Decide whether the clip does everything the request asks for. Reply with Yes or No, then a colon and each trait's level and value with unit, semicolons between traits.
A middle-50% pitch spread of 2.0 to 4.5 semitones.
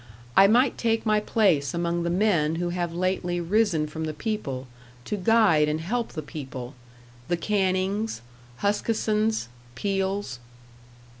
No: average, 4.9 semitones